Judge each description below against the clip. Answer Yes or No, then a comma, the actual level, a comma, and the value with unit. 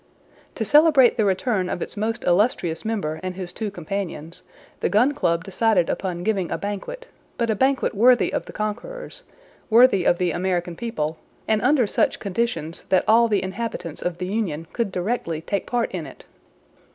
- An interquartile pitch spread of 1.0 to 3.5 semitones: No, average, 4.8 semitones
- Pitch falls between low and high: No, high, 200 Hz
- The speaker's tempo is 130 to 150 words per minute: No, average, 175 wpm